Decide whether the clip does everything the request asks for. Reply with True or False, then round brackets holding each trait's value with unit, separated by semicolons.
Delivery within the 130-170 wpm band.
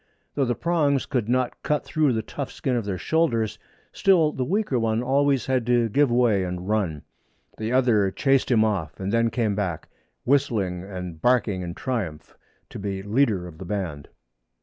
False (180 wpm)